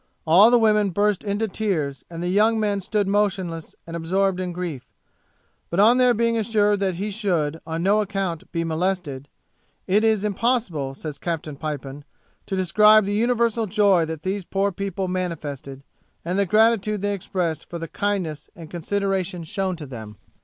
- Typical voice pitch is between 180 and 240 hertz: Yes, high, 190 Hz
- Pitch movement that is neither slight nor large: Yes, average, 4.0 semitones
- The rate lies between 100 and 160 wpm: No, average, 170 wpm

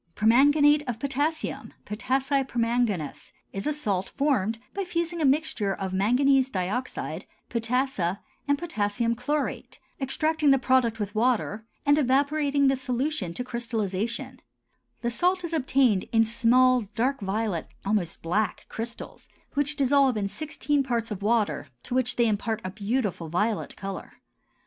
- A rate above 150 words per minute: No, average, 140 wpm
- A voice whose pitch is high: Yes, high, 245 Hz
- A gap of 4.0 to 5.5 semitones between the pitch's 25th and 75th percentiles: Yes, average, 4.7 semitones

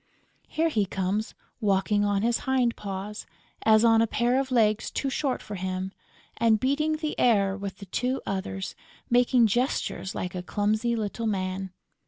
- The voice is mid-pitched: No, high, 215 Hz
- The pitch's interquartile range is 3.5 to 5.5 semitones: Yes, average, 3.8 semitones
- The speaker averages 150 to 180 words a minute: Yes, average, 165 wpm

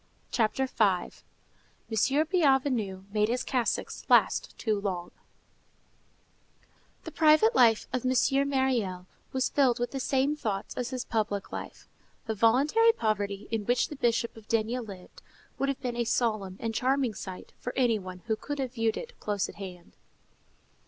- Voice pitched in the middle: No, high, 235 Hz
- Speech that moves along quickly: No, average, 155 wpm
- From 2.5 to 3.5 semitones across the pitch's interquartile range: No, average, 4.1 semitones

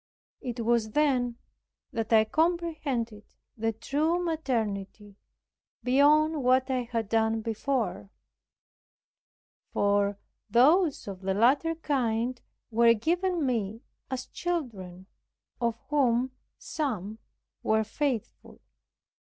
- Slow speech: Yes, slow, 95 wpm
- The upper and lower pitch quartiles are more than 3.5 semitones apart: Yes, average, 4.9 semitones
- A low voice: No, high, 240 Hz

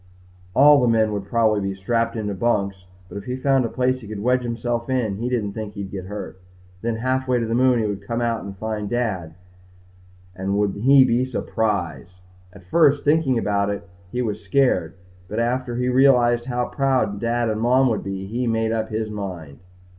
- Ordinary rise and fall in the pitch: Yes, average, 3.6 semitones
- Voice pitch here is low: Yes, low, 115 Hz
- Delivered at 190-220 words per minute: Yes, average, 200 wpm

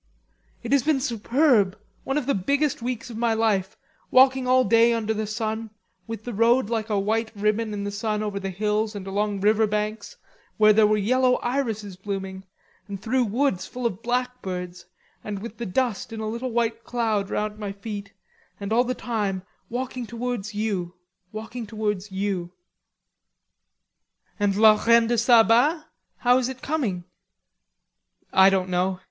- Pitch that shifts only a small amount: No, average, 3.1 semitones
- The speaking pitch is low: No, high, 220 Hz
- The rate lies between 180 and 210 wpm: No, average, 165 wpm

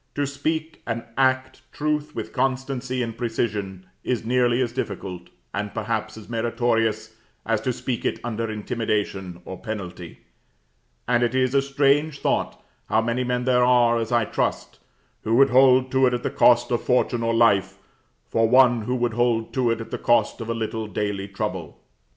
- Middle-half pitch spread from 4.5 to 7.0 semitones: No, narrow, 2.6 semitones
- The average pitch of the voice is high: No, low, 120 Hz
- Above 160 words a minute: Yes, average, 180 wpm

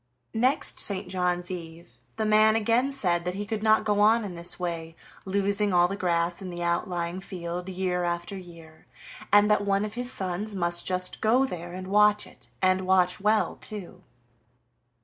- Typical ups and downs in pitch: Yes, average, 3.1 semitones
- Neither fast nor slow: Yes, average, 180 wpm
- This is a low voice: No, medium, 185 Hz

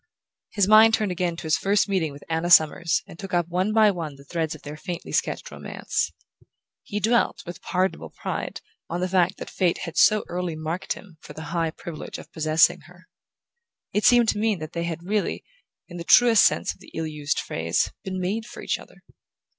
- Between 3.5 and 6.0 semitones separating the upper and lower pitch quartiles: Yes, average, 3.9 semitones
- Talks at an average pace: No, fast, 210 wpm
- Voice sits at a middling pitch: Yes, medium, 175 Hz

